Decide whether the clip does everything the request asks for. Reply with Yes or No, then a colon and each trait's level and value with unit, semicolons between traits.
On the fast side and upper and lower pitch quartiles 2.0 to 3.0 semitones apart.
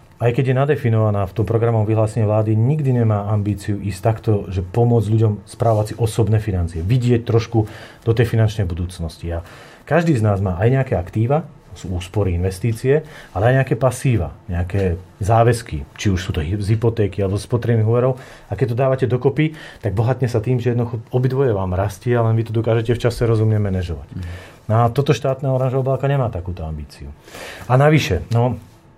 No: fast, 180 wpm; average, 3.7 semitones